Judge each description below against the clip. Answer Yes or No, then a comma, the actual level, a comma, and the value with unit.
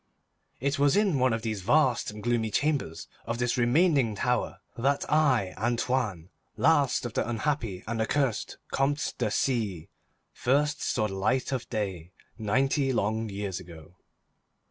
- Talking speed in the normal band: Yes, average, 145 wpm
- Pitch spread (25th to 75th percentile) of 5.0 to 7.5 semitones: No, average, 4.5 semitones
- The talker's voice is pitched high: No, low, 120 Hz